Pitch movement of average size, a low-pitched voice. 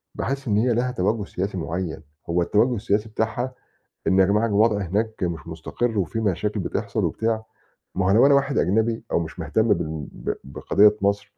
Yes: average, 3.7 semitones; low, 105 Hz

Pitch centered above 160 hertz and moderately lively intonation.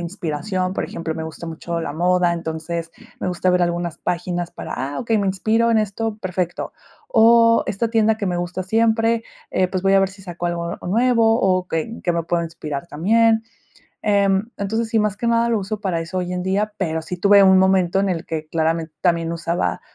Yes: medium, 185 Hz; average, 3.9 semitones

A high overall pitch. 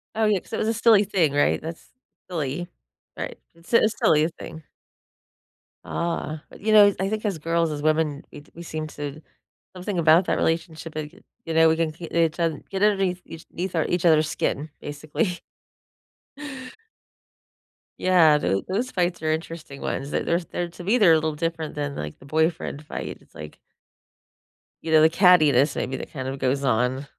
No: medium, 160 Hz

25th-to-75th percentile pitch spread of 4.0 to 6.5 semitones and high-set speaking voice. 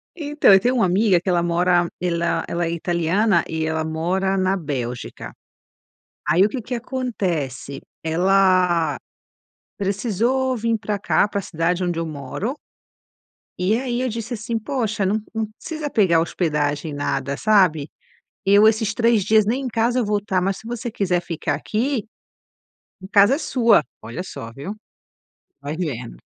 Yes: average, 5.0 semitones; high, 195 Hz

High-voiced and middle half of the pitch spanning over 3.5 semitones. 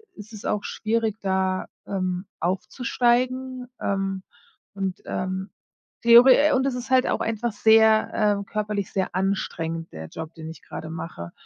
Yes: high, 200 Hz; average, 4.0 semitones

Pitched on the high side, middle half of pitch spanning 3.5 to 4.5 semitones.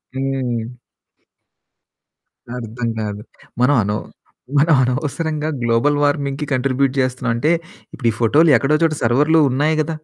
No: low, 135 Hz; average, 3.8 semitones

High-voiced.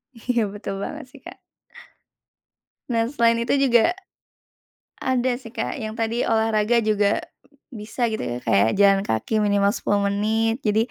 Yes: high, 220 Hz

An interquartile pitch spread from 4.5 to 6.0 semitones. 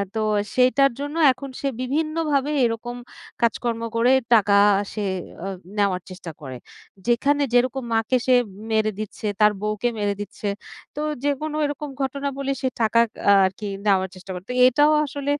Yes: average, 4.8 semitones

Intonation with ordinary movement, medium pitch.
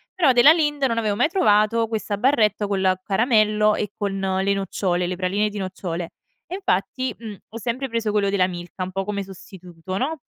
No: average, 3.4 semitones; high, 210 Hz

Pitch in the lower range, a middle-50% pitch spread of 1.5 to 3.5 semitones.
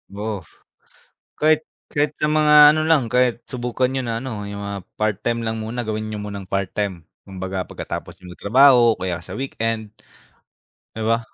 No: low, 110 Hz; average, 3.9 semitones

